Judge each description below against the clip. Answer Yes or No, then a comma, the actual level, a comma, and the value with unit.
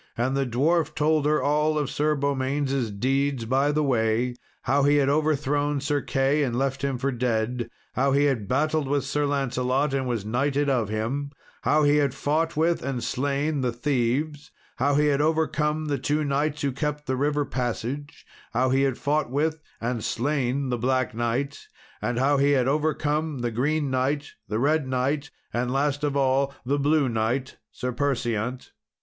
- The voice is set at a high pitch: No, medium, 140 Hz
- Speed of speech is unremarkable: Yes, average, 180 wpm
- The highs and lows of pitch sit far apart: No, narrow, 2.6 semitones